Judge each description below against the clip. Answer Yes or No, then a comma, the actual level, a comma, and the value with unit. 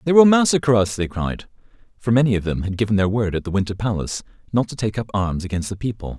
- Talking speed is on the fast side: Yes, fast, 250 wpm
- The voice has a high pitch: No, low, 105 Hz